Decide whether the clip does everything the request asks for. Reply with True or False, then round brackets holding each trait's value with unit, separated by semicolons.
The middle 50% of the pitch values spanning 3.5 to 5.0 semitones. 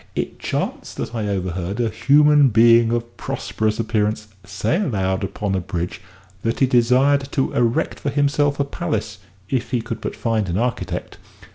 True (4.6 semitones)